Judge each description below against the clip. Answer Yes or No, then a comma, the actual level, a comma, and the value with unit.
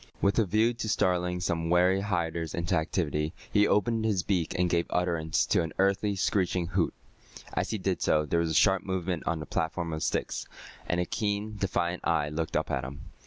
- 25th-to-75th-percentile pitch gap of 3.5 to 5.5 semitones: No, average, 3.0 semitones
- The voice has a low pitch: Yes, very low, 90 Hz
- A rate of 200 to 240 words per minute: Yes, fast, 205 wpm